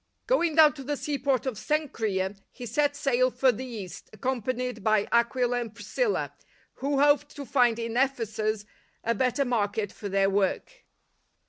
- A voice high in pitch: Yes, high, 245 Hz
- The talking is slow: No, average, 160 wpm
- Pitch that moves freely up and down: No, average, 4.3 semitones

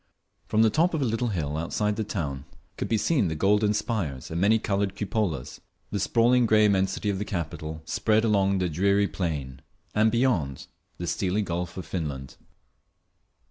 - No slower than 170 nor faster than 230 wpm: Yes, average, 175 wpm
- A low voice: Yes, low, 100 Hz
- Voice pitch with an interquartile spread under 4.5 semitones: No, average, 4.9 semitones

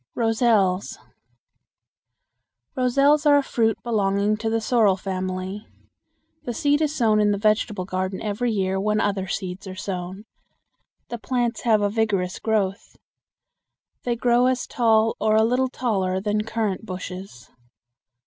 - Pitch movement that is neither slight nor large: Yes, average, 3.6 semitones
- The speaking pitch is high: Yes, high, 215 Hz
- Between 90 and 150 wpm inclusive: Yes, average, 140 wpm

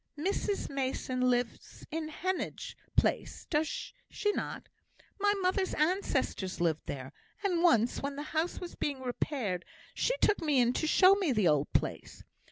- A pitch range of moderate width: No, wide, 7.1 semitones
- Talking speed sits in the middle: Yes, average, 155 wpm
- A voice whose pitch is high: Yes, very high, 295 Hz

